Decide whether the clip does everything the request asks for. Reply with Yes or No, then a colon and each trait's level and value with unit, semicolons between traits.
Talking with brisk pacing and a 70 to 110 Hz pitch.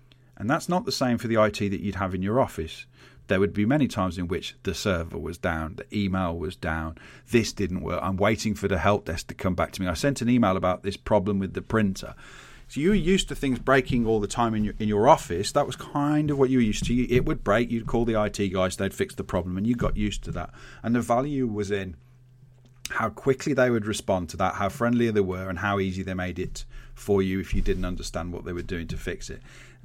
Yes: fast, 260 wpm; low, 105 Hz